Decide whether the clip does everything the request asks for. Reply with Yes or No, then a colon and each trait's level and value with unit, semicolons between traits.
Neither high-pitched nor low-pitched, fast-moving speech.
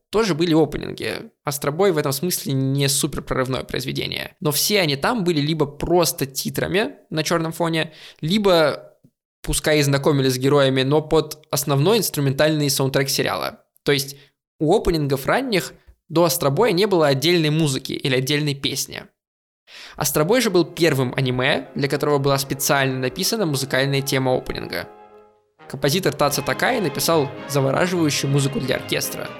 No: medium, 145 Hz; average, 140 wpm